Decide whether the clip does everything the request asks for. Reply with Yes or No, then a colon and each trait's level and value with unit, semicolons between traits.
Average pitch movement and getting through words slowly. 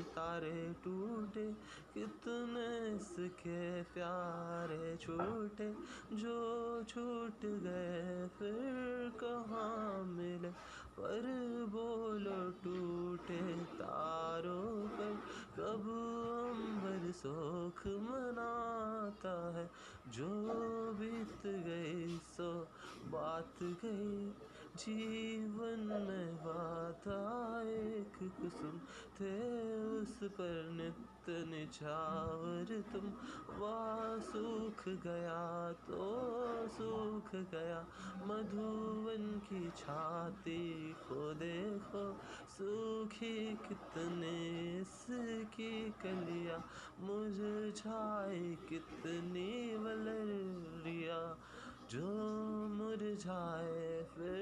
Yes: average, 4.4 semitones; slow, 60 wpm